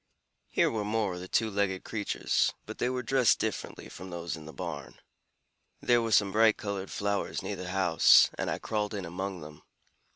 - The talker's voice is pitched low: Yes, low, 100 Hz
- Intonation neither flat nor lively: Yes, average, 3.2 semitones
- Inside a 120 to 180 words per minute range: No, average, 195 wpm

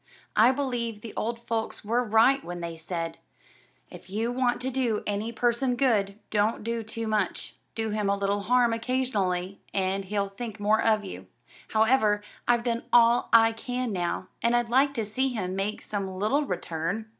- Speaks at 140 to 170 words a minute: No, average, 180 wpm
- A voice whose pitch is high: Yes, high, 220 Hz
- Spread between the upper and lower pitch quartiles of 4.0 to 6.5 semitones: No, average, 3.3 semitones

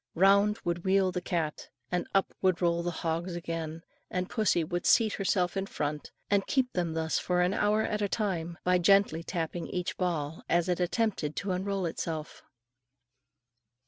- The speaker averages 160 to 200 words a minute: Yes, average, 175 wpm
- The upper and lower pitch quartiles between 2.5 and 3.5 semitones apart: Yes, average, 2.8 semitones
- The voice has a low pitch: No, medium, 180 Hz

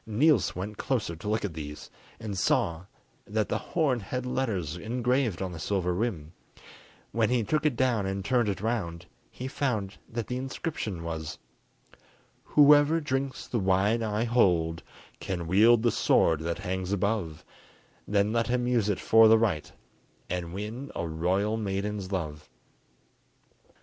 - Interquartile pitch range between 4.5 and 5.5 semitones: Yes, average, 5.0 semitones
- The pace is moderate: Yes, average, 155 wpm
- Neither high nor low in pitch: No, low, 105 Hz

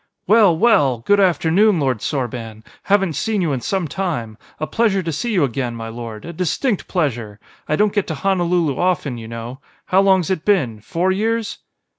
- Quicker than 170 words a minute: Yes, average, 185 wpm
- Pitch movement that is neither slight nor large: No, wide, 7.8 semitones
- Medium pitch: Yes, medium, 165 Hz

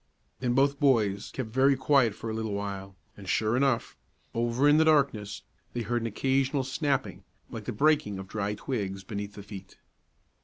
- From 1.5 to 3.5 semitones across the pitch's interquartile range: No, average, 4.8 semitones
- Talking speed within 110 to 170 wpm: No, average, 180 wpm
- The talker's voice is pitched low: Yes, low, 115 Hz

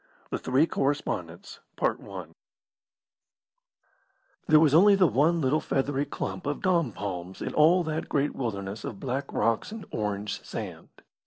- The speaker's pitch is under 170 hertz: Yes, medium, 140 Hz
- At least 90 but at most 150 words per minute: Yes, slow, 135 wpm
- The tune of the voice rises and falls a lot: Yes, wide, 6.6 semitones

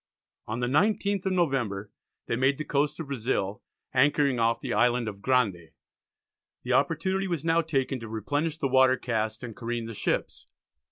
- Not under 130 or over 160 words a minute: No, average, 170 wpm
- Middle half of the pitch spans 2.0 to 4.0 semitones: No, average, 4.9 semitones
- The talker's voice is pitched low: Yes, low, 130 Hz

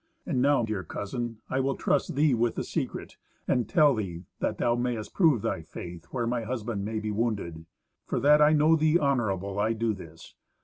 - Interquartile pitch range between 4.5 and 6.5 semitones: Yes, average, 5.0 semitones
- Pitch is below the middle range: Yes, low, 115 Hz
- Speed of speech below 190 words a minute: No, average, 195 wpm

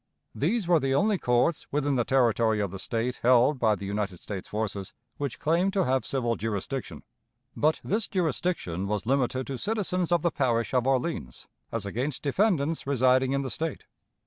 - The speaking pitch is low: Yes, low, 130 Hz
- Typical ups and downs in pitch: No, wide, 5.8 semitones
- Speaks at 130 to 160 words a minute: No, average, 175 wpm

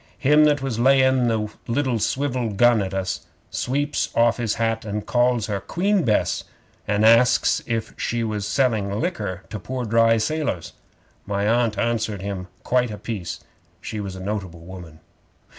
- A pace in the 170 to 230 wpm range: No, average, 160 wpm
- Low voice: Yes, low, 115 Hz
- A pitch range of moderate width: Yes, average, 3.7 semitones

